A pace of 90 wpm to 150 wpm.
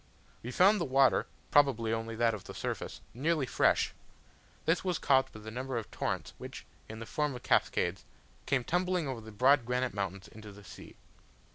No: average, 185 wpm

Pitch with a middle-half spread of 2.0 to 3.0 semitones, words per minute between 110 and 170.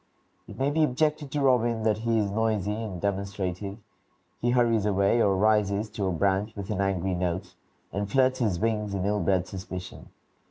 No: average, 2.7 semitones; average, 185 wpm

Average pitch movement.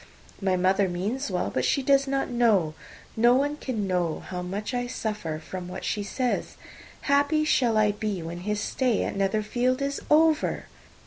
No: wide, 5.7 semitones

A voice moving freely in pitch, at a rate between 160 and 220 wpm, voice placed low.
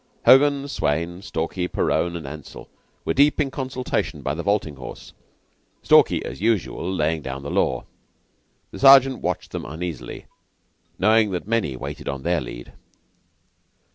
No: wide, 7.2 semitones; average, 140 wpm; very low, 90 Hz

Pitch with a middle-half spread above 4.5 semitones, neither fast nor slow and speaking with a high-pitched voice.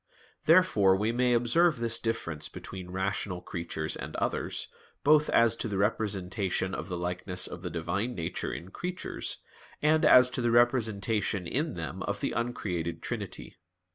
No: average, 5.2 semitones; average, 155 wpm; low, 100 Hz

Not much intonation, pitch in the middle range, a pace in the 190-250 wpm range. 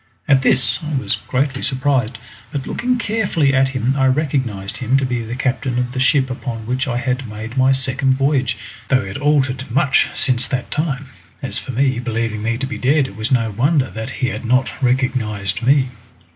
No: narrow, 2.1 semitones; low, 130 Hz; average, 200 wpm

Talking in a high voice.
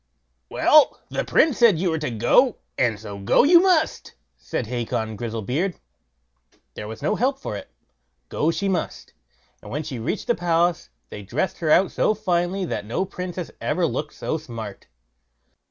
No: medium, 165 Hz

